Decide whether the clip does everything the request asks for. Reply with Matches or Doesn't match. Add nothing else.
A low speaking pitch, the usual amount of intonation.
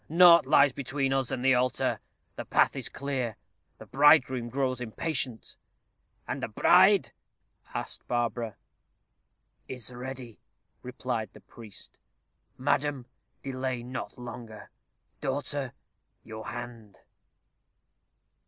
Doesn't match